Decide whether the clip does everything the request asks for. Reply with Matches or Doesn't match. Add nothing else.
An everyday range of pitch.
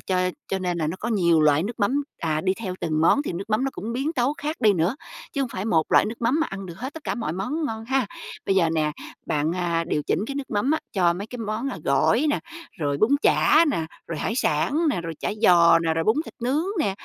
Doesn't match